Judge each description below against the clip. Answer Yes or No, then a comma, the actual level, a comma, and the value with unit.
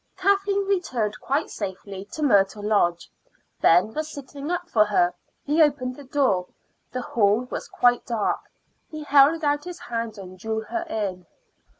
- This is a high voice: Yes, high, 245 Hz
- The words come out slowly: No, average, 160 wpm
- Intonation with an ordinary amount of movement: No, wide, 6.9 semitones